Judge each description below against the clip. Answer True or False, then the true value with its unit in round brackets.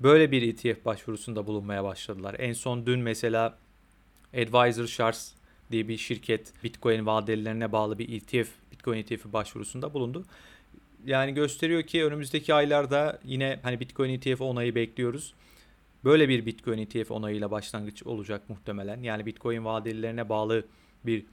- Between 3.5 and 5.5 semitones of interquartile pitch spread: False (2.6 semitones)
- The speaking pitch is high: False (115 Hz)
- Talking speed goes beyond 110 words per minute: True (135 wpm)